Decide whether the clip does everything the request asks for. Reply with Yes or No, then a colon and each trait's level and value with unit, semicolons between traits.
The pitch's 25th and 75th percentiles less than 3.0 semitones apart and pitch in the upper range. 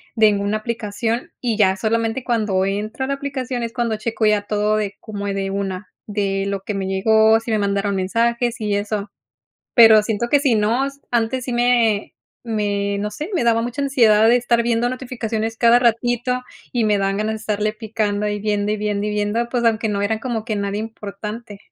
Yes: narrow, 2.4 semitones; high, 220 Hz